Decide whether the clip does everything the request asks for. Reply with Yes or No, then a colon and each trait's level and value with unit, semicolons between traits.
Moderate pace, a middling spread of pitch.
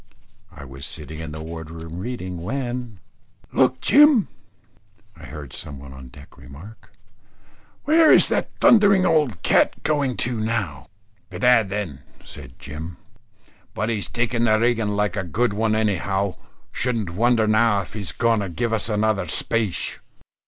No: average, 155 wpm; wide, 6.1 semitones